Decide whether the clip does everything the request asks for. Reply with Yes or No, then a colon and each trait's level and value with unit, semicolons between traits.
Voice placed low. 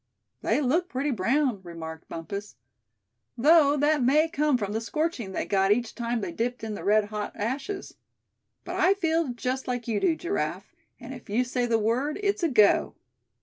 No: high, 245 Hz